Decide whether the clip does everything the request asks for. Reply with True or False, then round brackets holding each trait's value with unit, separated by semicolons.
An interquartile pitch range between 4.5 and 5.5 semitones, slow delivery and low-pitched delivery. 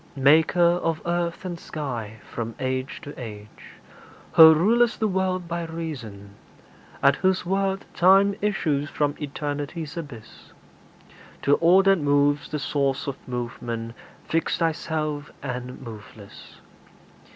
False (4.9 semitones; 120 wpm; 150 Hz)